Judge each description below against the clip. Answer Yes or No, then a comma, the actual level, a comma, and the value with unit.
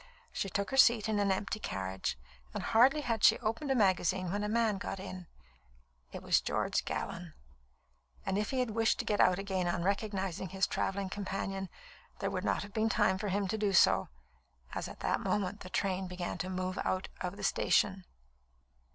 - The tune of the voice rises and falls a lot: No, narrow, 2.4 semitones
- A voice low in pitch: No, high, 195 Hz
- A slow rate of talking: No, average, 195 wpm